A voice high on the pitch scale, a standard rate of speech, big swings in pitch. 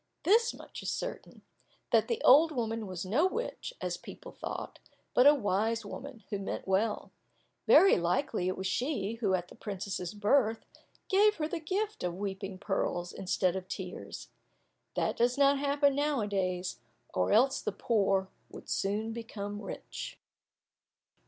Yes: high, 215 Hz; average, 160 wpm; wide, 6.7 semitones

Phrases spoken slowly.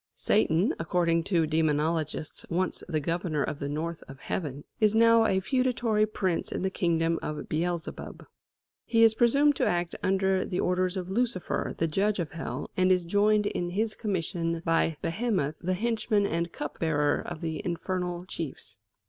No: average, 165 wpm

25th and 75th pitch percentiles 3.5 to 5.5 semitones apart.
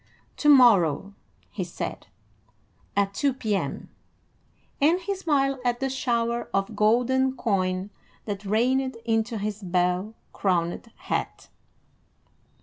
Yes: average, 4.9 semitones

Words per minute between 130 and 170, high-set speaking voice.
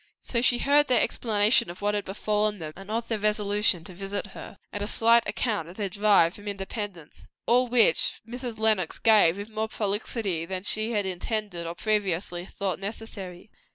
No: average, 185 wpm; high, 205 Hz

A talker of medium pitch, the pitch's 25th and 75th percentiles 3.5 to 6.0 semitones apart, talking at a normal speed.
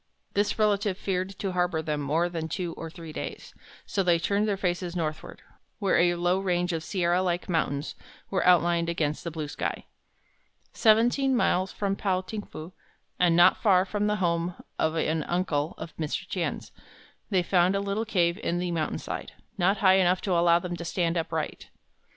No: medium, 175 Hz; narrow, 2.5 semitones; average, 180 wpm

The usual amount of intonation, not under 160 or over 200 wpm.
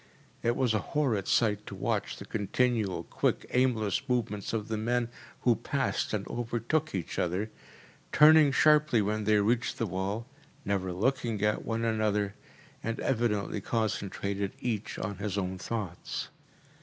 No: average, 3.0 semitones; average, 145 wpm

